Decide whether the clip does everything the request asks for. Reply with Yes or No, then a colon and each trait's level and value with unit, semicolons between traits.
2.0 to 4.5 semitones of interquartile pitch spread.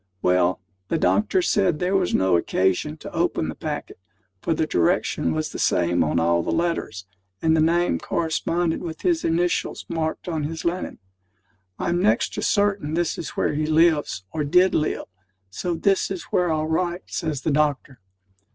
Yes: average, 3.8 semitones